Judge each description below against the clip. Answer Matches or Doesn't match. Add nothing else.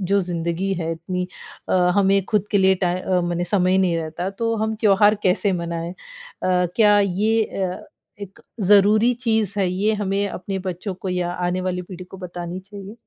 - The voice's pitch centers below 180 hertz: Doesn't match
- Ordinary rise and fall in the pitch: Doesn't match